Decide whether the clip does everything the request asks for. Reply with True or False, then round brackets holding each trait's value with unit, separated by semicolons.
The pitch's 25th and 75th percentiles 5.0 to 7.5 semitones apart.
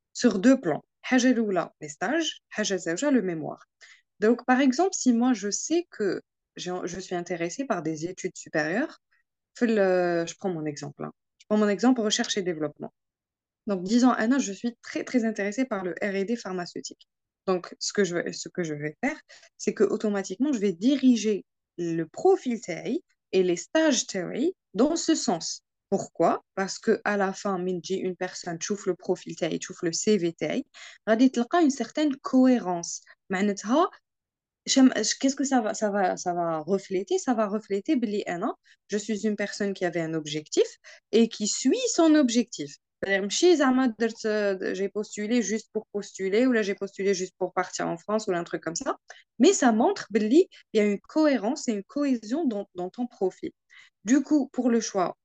True (5.5 semitones)